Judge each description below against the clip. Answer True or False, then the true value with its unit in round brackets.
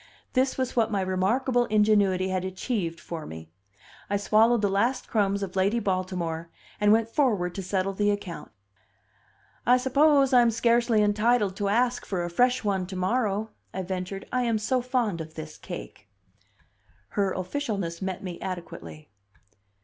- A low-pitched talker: False (205 Hz)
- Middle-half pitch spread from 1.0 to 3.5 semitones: False (4.3 semitones)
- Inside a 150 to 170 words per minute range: True (155 wpm)